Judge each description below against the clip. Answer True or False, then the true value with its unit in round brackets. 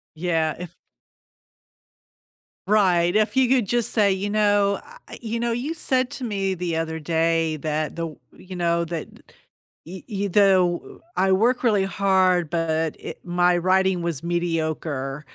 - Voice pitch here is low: False (180 Hz)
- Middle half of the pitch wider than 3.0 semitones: True (3.7 semitones)